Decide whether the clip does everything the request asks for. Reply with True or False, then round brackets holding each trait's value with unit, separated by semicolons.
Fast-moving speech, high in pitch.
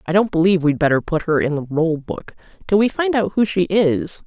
False (255 wpm; 180 Hz)